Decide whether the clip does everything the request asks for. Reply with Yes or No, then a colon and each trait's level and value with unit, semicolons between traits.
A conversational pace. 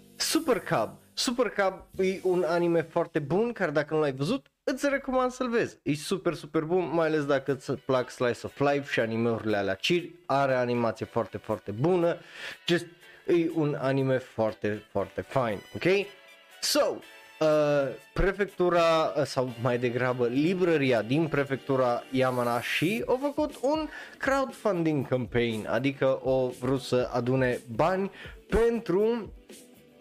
Yes: average, 140 wpm